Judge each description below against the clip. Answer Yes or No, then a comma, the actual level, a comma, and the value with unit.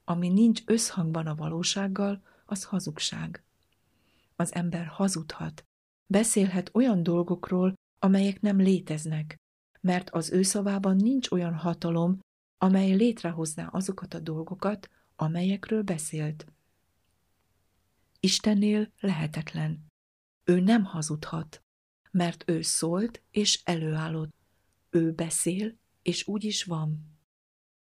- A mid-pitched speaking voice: Yes, medium, 175 Hz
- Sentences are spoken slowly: Yes, slow, 100 wpm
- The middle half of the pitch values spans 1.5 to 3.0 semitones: No, average, 3.8 semitones